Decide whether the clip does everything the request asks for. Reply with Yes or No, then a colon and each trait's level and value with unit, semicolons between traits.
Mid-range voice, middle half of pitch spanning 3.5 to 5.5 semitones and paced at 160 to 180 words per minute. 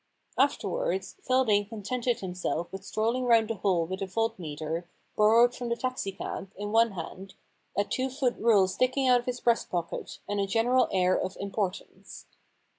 No: high, 215 Hz; average, 4.3 semitones; average, 170 wpm